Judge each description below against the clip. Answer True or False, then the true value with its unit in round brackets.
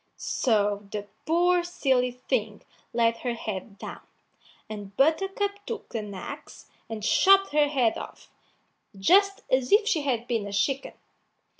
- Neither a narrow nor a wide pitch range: False (8.5 semitones)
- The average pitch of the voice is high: True (255 Hz)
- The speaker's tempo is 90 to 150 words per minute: True (140 wpm)